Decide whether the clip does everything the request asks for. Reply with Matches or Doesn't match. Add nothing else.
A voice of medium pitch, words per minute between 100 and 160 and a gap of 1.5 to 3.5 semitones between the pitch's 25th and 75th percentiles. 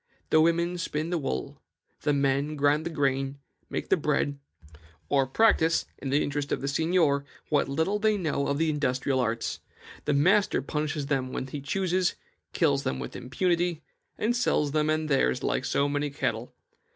Doesn't match